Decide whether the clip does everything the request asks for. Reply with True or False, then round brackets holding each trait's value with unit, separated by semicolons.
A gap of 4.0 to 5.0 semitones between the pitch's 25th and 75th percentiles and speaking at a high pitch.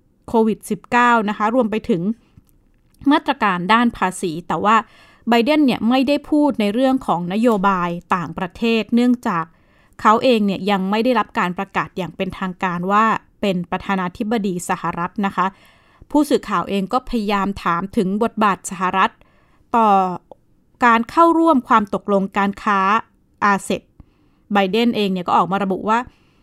False (3.6 semitones; 210 Hz)